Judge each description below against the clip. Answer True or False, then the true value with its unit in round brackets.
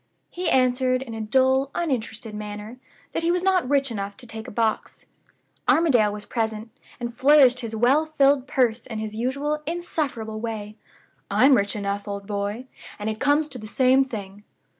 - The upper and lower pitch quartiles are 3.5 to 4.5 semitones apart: True (4.0 semitones)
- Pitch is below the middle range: False (240 Hz)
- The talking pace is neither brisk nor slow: True (175 wpm)